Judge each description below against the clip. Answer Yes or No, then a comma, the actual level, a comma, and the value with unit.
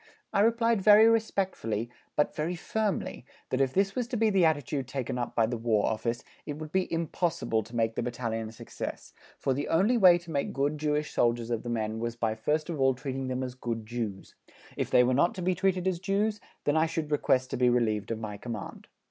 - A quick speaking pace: Yes, fast, 225 wpm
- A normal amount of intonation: No, wide, 7.3 semitones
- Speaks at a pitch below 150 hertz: Yes, medium, 140 Hz